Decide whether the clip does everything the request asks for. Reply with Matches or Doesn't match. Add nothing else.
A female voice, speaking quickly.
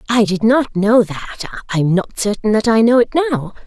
Matches